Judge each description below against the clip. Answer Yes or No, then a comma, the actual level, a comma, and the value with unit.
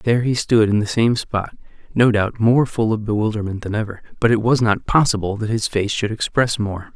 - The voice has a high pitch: No, low, 110 Hz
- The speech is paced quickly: Yes, fast, 225 wpm